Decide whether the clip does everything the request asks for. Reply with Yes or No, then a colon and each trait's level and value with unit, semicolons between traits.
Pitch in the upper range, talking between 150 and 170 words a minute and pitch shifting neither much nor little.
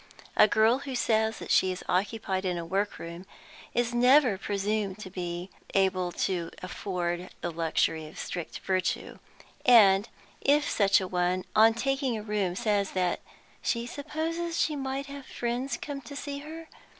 No: high, 210 Hz; average, 160 wpm; wide, 6.0 semitones